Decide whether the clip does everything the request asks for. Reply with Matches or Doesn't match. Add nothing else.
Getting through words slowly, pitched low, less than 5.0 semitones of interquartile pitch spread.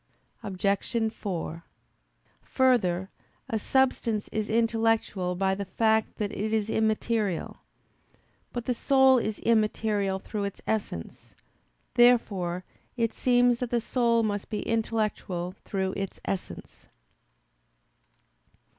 Doesn't match